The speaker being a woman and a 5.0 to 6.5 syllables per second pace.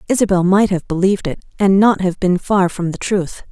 Yes: female; 5.5 syllables/s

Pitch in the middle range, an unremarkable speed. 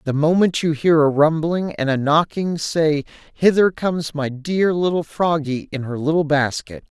Yes: medium, 155 Hz; average, 170 wpm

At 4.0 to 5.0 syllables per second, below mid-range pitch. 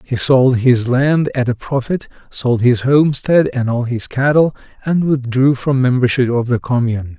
Yes: 4.6 syllables/s; low, 125 Hz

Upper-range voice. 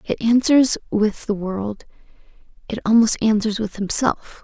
Yes: high, 215 Hz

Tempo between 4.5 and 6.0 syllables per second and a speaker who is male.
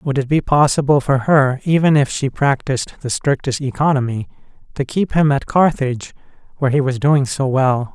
Yes: 5.2 syllables/s; male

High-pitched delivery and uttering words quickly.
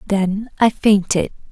No: high, 205 Hz; slow, 120 wpm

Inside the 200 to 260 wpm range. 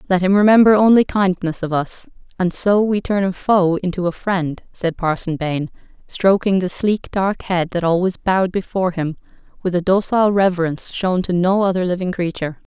No: average, 185 wpm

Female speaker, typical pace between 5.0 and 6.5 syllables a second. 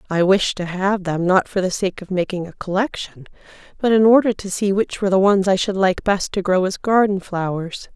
Yes: female; 5.3 syllables/s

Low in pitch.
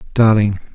Yes: low, 105 Hz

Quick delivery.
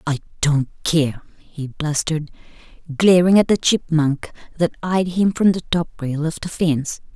No: average, 160 wpm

